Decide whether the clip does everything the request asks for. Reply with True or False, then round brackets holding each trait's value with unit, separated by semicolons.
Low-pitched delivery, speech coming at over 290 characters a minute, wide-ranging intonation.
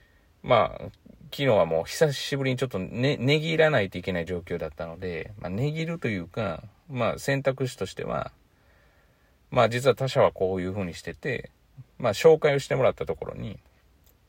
True (115 Hz; 355 characters per minute; 8.0 semitones)